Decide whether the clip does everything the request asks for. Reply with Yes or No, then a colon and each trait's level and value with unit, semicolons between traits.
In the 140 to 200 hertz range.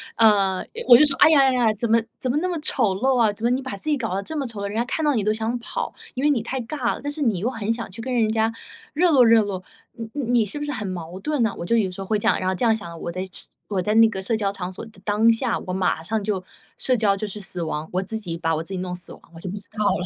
No: high, 220 Hz